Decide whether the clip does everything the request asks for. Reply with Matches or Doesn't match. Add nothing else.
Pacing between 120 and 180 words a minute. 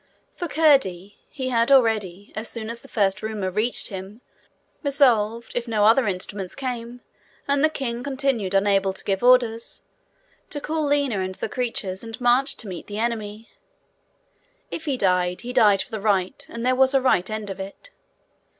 Matches